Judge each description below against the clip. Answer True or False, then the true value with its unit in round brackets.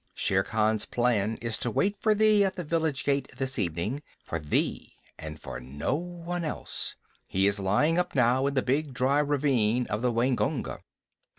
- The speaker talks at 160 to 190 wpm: True (180 wpm)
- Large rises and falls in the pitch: True (6.1 semitones)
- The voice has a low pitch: True (130 Hz)